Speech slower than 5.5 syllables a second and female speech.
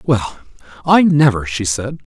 No: 4.7 syllables/s; male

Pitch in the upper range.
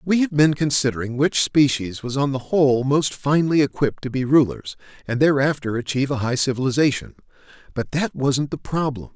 No: low, 135 Hz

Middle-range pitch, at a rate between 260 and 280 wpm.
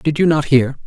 Yes: medium, 145 Hz; fast, 275 wpm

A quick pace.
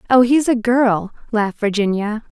No: average, 150 wpm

